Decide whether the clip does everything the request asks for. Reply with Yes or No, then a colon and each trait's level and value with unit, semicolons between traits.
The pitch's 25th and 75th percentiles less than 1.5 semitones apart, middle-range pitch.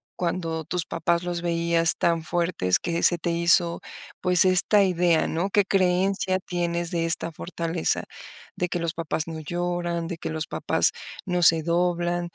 Yes: narrow, 1.1 semitones; medium, 170 Hz